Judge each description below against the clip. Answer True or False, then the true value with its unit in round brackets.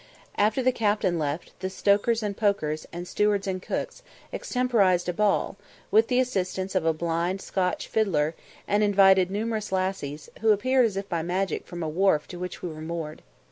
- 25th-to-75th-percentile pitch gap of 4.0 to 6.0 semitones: False (3.3 semitones)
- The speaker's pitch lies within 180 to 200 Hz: True (190 Hz)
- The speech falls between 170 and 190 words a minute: True (180 wpm)